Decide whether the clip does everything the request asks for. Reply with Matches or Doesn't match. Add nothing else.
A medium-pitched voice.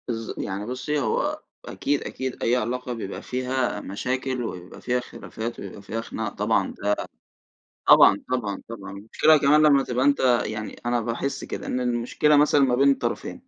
Doesn't match